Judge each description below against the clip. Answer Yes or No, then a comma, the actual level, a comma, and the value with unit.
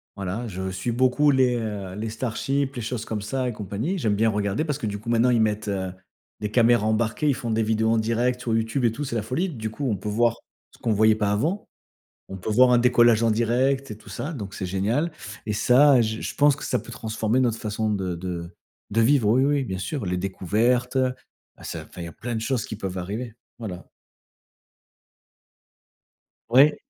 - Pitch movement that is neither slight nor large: Yes, average, 3.2 semitones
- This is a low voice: Yes, low, 115 Hz